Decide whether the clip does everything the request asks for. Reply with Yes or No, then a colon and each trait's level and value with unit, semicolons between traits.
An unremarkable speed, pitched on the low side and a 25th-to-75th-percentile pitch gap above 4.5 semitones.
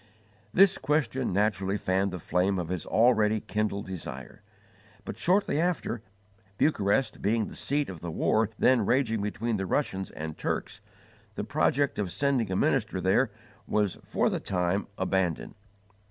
Yes: average, 150 wpm; low, 105 Hz; average, 5.1 semitones